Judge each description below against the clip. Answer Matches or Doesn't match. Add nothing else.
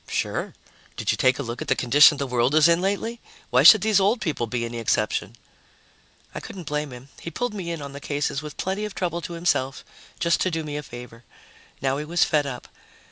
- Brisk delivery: Matches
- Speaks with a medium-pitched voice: Matches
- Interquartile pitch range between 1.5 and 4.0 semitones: Doesn't match